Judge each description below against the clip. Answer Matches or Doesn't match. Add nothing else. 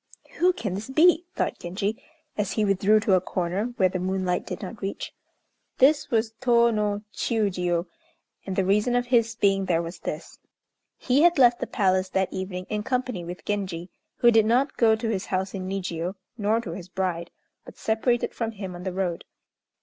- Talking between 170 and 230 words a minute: Matches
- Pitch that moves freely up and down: Doesn't match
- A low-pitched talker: Doesn't match